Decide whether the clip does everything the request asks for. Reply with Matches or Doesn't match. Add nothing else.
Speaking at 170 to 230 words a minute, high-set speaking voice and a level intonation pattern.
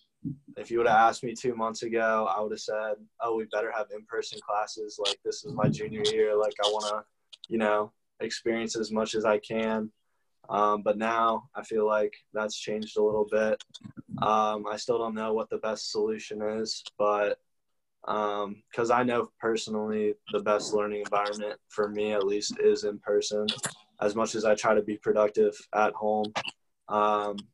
Doesn't match